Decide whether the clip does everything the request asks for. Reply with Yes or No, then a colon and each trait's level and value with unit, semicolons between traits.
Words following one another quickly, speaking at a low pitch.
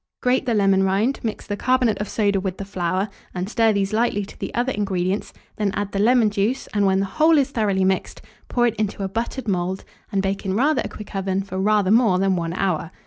No: fast, 235 wpm; high, 200 Hz